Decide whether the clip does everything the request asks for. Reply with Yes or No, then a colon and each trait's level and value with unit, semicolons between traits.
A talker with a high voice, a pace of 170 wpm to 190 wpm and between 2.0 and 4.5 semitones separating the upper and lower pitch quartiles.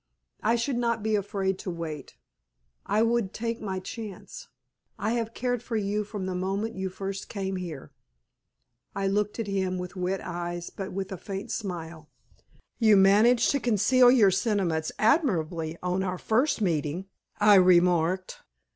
No: high, 195 Hz; average, 160 wpm; average, 3.6 semitones